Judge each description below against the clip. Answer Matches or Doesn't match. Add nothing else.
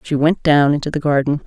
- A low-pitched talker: Doesn't match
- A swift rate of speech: Matches